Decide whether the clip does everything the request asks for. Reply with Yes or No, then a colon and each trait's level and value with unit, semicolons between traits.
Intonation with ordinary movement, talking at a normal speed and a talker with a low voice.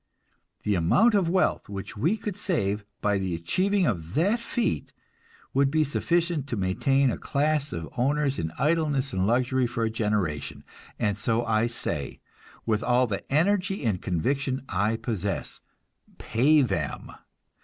No: wide, 7.0 semitones; average, 150 wpm; low, 125 Hz